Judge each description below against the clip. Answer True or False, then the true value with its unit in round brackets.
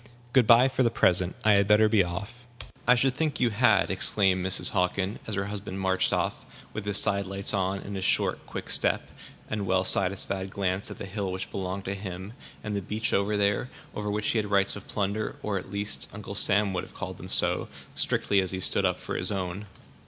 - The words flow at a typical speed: False (215 wpm)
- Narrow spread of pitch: True (1.9 semitones)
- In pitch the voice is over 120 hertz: False (100 Hz)